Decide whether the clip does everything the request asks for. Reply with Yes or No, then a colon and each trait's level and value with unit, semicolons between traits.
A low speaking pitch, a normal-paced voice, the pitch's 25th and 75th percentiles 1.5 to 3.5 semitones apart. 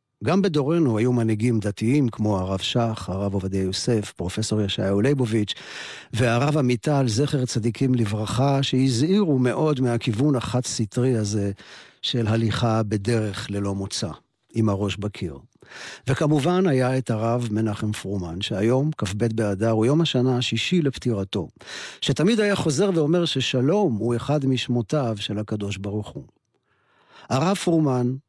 No: low, 120 Hz; average, 130 wpm; average, 4.2 semitones